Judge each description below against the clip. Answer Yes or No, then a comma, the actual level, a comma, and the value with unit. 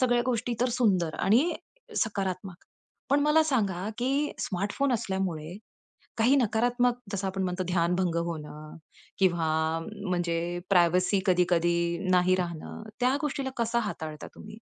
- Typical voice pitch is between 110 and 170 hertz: No, high, 190 Hz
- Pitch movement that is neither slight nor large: No, wide, 5.7 semitones